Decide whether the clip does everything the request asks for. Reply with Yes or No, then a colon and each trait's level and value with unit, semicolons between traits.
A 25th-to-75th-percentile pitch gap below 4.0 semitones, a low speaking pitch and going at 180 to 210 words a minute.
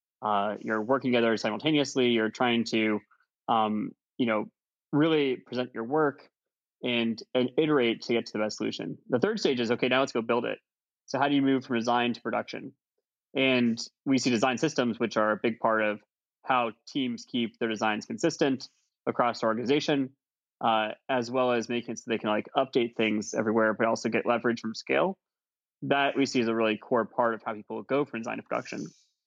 Yes: average, 3.1 semitones; low, 120 Hz; average, 200 wpm